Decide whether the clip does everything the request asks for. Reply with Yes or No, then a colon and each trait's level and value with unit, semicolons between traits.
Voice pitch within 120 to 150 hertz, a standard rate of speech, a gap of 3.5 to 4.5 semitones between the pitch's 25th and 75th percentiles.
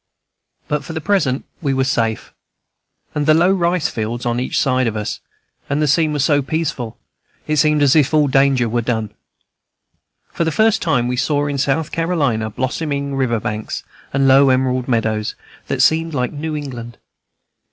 Yes: medium, 140 Hz; average, 175 wpm; average, 3.9 semitones